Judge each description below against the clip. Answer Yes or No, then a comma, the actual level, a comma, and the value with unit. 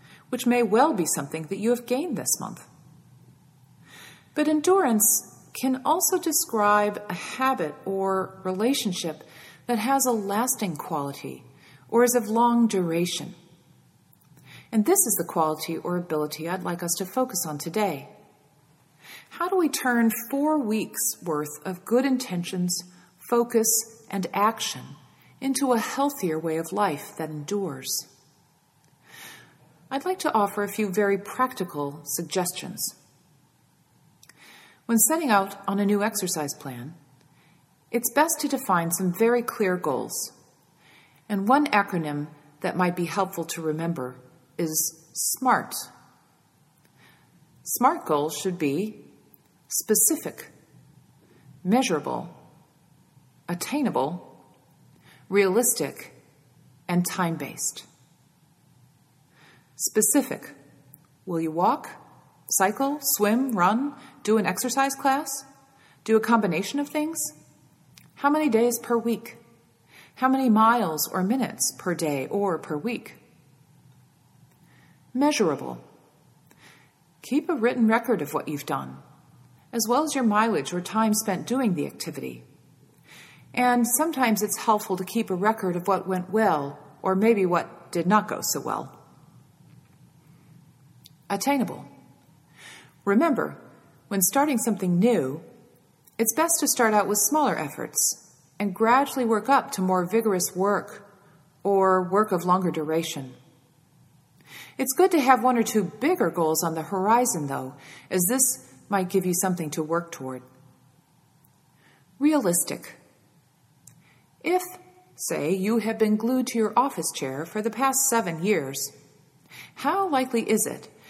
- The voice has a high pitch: Yes, high, 195 Hz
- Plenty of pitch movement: Yes, wide, 7.1 semitones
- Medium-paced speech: No, slow, 125 wpm